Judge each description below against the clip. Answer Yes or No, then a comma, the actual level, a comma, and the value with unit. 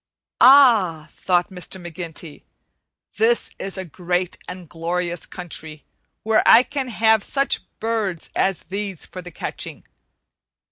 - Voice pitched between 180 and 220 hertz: Yes, medium, 185 Hz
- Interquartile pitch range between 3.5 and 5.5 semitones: Yes, average, 4.2 semitones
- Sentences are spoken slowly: Yes, slow, 125 wpm